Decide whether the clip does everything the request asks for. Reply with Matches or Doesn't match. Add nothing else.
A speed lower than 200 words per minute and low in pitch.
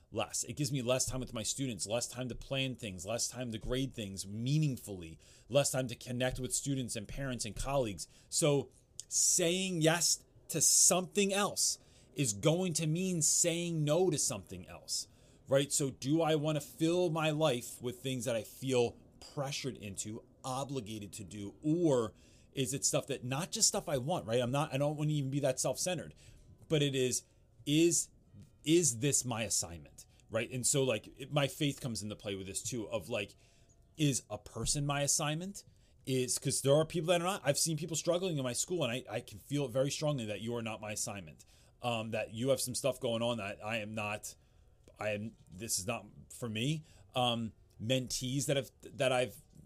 Doesn't match